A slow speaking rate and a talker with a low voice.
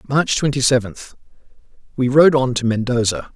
Yes: slow, 125 wpm; low, 130 Hz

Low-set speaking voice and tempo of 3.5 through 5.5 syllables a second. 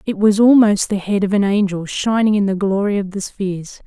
No: high, 200 Hz; 5.4 syllables/s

